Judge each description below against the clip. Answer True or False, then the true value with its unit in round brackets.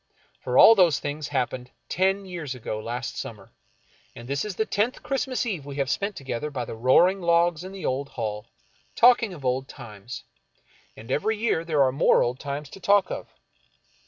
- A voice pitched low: False (145 Hz)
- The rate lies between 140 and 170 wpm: False (190 wpm)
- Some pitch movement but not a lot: False (7.0 semitones)